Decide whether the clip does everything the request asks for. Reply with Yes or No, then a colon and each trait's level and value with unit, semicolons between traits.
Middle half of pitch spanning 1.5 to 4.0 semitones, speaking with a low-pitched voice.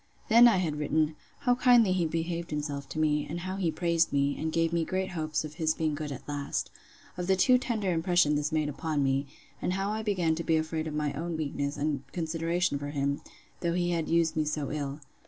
No: average, 2.9 semitones; medium, 160 Hz